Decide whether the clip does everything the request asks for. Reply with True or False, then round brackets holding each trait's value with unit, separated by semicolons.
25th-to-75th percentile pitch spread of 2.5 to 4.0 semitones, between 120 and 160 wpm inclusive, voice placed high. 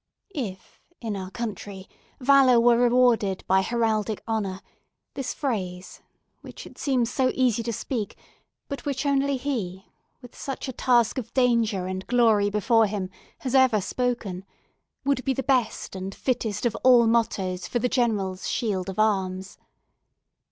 False (4.4 semitones; 145 wpm; 230 Hz)